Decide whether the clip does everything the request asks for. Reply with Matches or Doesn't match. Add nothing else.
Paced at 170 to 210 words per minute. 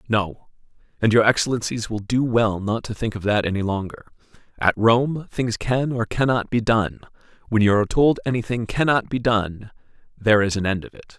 Matches